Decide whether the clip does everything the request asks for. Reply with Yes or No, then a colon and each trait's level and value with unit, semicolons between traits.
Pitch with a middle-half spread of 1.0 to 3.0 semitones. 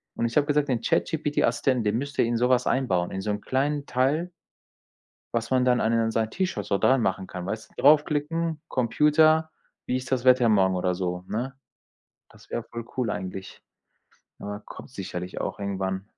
No: wide, 5.5 semitones